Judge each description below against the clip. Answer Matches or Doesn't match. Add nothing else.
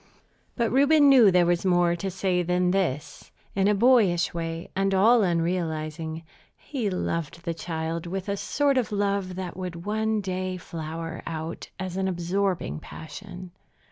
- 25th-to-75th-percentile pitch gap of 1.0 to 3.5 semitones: Matches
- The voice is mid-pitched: Matches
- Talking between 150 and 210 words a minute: Matches